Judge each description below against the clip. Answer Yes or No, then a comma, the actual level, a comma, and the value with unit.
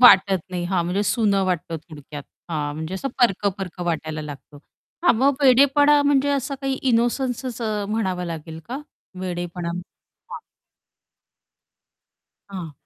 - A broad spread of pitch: Yes, wide, 7.0 semitones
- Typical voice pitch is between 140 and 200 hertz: Yes, high, 190 Hz